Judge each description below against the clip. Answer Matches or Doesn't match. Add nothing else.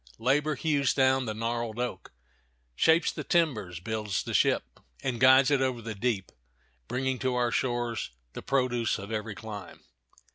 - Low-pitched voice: Matches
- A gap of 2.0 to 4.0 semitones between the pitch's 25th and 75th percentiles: Matches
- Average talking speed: Matches